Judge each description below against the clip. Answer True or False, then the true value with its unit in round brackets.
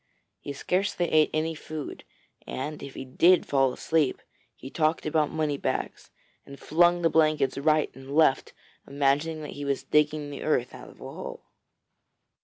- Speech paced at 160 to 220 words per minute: True (165 wpm)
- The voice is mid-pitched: True (150 Hz)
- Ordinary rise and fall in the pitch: False (2.2 semitones)